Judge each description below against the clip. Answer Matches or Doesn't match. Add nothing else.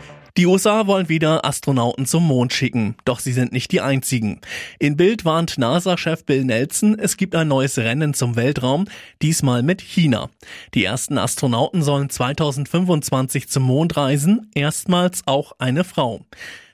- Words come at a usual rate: Matches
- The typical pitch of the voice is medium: Matches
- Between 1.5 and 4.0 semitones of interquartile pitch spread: Doesn't match